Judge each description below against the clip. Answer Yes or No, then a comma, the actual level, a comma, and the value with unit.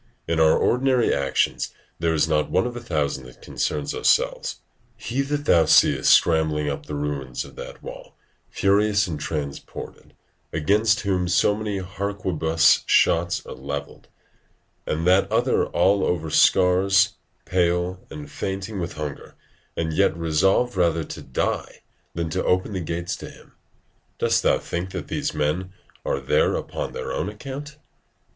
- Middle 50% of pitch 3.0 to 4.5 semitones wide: Yes, average, 4.1 semitones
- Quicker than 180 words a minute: No, average, 150 wpm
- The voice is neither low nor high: No, very low, 85 Hz